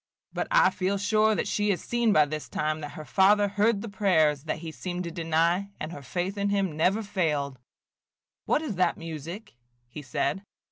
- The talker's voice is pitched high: No, medium, 180 Hz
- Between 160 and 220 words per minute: Yes, average, 195 wpm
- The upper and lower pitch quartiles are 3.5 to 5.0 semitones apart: Yes, average, 4.6 semitones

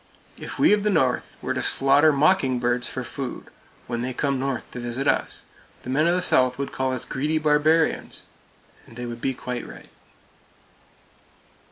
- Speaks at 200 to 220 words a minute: No, average, 175 wpm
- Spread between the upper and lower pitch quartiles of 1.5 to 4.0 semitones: Yes, average, 3.4 semitones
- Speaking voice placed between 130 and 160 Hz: Yes, low, 135 Hz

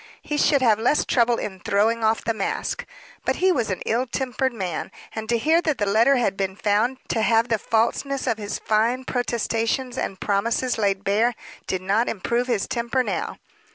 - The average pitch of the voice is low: No, high, 230 Hz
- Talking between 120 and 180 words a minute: No, average, 190 wpm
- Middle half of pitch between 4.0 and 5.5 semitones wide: No, average, 3.2 semitones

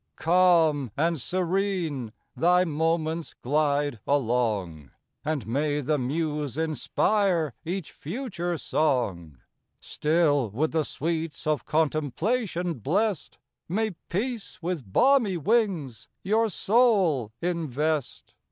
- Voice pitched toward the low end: No, medium, 160 Hz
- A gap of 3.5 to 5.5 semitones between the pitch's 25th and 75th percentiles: Yes, average, 4.3 semitones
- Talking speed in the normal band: No, slow, 95 wpm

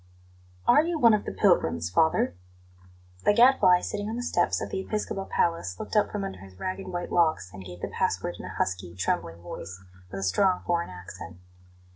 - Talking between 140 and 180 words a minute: No, average, 195 wpm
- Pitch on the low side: No, medium, 170 Hz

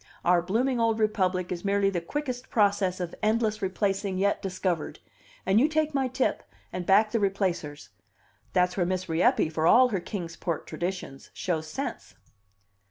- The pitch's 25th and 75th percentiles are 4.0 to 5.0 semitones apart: No, average, 3.5 semitones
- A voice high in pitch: Yes, high, 195 Hz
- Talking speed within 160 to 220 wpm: Yes, average, 165 wpm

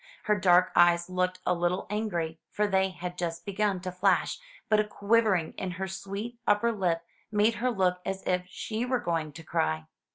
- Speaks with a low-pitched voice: No, medium, 185 Hz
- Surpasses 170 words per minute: Yes, average, 190 wpm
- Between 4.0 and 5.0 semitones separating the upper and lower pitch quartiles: No, average, 3.1 semitones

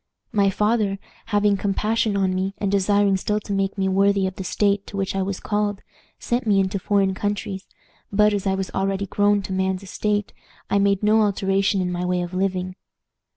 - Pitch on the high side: Yes, high, 195 Hz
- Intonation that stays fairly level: Yes, narrow, 1.3 semitones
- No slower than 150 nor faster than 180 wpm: No, average, 200 wpm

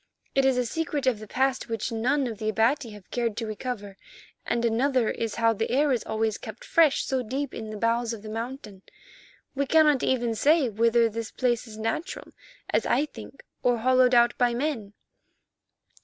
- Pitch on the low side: No, high, 235 Hz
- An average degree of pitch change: Yes, average, 3.0 semitones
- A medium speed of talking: Yes, average, 190 wpm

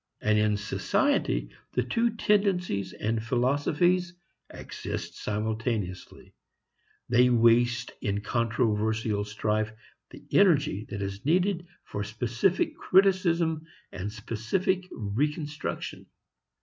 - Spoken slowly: Yes, slow, 95 wpm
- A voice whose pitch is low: Yes, low, 120 Hz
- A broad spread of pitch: Yes, wide, 8.0 semitones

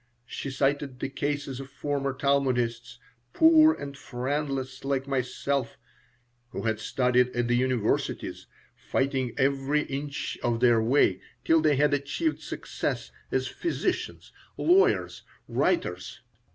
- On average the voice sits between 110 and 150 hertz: Yes, low, 135 Hz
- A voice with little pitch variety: Yes, narrow, 2.3 semitones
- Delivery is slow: Yes, slow, 120 wpm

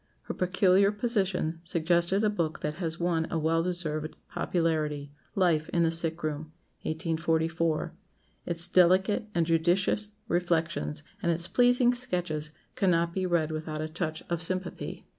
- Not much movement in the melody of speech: Yes, narrow, 2.3 semitones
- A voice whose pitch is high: No, medium, 170 Hz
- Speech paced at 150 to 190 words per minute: No, average, 140 wpm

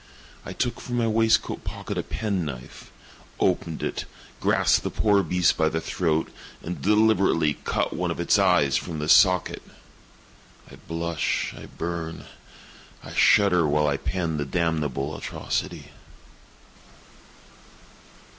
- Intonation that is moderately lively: Yes, average, 3.7 semitones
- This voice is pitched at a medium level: No, very low, 85 Hz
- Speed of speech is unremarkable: No, slow, 130 wpm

